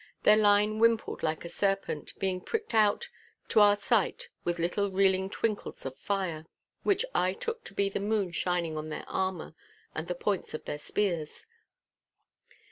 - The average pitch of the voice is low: No, high, 195 Hz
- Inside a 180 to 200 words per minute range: No, average, 165 wpm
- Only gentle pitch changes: No, average, 3.4 semitones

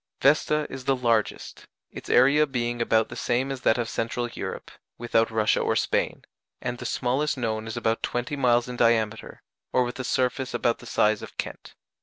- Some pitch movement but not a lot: No, narrow, 2.2 semitones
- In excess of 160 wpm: Yes, average, 190 wpm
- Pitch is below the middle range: Yes, low, 120 Hz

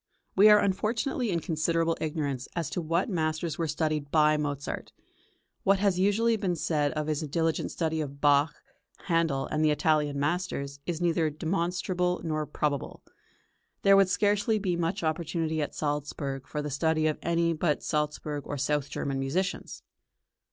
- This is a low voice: No, medium, 160 Hz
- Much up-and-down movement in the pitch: No, average, 3.1 semitones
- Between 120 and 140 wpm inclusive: No, average, 160 wpm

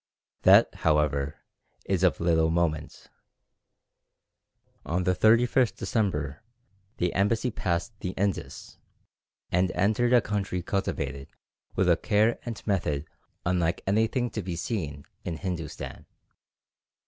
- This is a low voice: Yes, very low, 90 Hz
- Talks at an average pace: No, slow, 110 wpm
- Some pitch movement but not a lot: Yes, average, 4.5 semitones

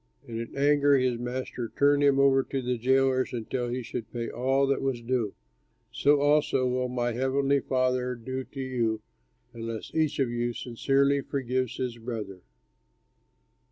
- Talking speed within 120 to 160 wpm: Yes, average, 155 wpm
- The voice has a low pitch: Yes, low, 130 Hz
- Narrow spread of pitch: Yes, narrow, 2.3 semitones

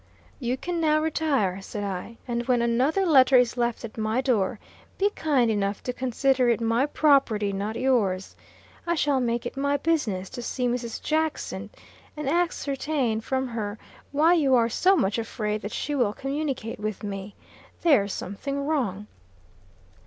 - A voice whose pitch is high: Yes, high, 245 Hz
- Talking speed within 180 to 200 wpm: No, average, 165 wpm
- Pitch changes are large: No, average, 4.7 semitones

